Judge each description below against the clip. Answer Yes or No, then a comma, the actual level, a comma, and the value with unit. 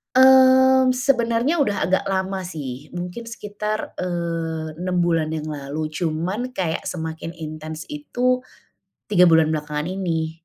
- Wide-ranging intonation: Yes, wide, 6.4 semitones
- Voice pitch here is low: No, medium, 175 Hz